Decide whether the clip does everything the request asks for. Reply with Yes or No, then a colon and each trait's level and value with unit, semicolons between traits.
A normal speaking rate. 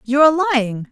Yes: average, 195 wpm